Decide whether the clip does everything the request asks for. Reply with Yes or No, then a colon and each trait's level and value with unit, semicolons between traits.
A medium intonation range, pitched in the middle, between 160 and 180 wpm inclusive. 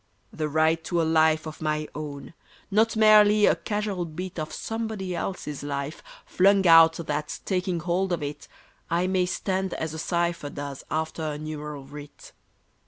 Yes: average, 3.5 semitones; medium, 165 Hz; average, 165 wpm